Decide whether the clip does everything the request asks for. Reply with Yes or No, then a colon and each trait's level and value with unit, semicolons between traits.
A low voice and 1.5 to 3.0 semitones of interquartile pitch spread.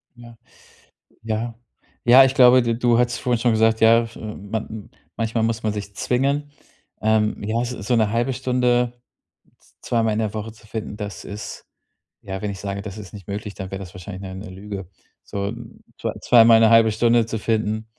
Yes: low, 110 Hz; narrow, 2.4 semitones